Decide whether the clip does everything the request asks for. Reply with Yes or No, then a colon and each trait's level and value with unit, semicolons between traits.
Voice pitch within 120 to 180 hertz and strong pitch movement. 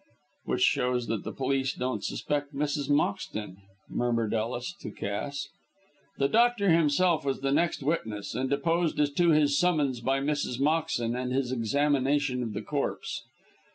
No: medium, 140 Hz; average, 3.3 semitones